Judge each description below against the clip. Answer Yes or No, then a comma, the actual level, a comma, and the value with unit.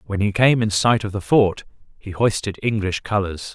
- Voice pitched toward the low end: Yes, low, 105 Hz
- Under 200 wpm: No, fast, 205 wpm